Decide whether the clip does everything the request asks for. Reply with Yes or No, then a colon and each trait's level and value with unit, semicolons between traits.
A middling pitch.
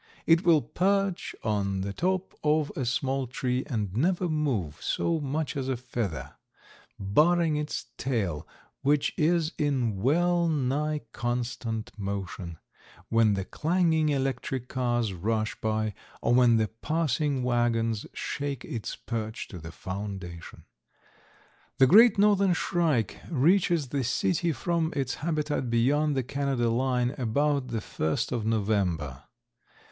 No: low, 130 Hz